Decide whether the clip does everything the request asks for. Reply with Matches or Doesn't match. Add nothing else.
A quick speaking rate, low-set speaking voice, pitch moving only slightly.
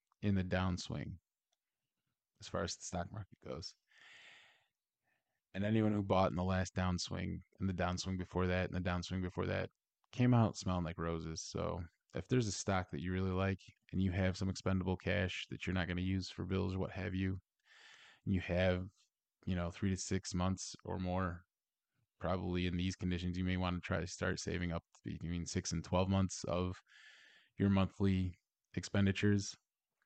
Doesn't match